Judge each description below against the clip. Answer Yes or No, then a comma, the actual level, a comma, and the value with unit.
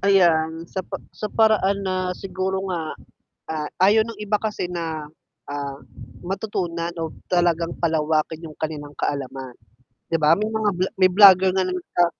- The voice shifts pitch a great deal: No, average, 3.4 semitones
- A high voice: No, medium, 175 Hz